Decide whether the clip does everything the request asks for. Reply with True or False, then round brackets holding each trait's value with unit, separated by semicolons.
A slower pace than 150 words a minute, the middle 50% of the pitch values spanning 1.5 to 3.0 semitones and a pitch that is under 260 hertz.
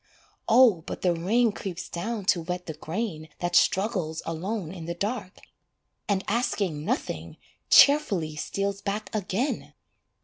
False (135 wpm; 4.3 semitones; 190 Hz)